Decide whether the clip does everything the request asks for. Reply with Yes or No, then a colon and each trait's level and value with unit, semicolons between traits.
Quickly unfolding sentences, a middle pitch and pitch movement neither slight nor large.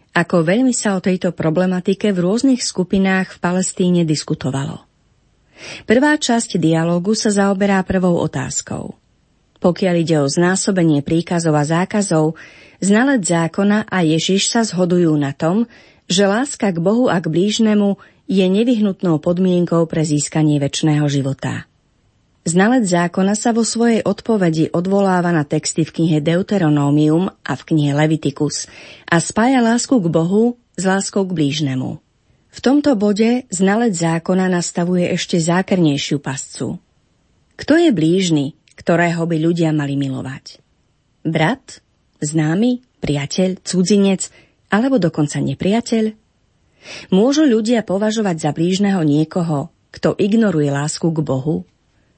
No: average, 125 wpm; medium, 180 Hz; average, 4.5 semitones